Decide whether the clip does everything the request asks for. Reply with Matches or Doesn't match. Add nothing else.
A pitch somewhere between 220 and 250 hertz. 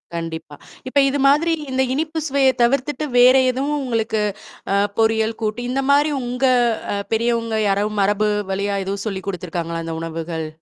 Matches